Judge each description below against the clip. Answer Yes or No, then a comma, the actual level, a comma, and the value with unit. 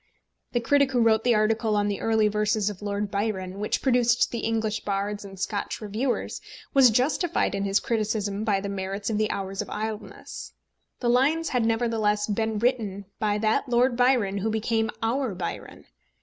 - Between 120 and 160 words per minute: No, average, 180 wpm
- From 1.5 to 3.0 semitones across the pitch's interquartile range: Yes, narrow, 2.6 semitones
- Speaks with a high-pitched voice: Yes, high, 215 Hz